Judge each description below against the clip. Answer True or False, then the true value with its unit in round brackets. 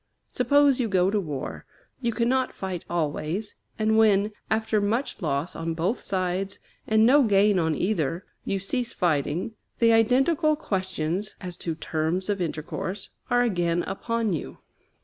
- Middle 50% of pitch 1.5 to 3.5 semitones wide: False (4.6 semitones)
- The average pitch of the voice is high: True (195 Hz)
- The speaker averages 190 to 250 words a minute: False (150 wpm)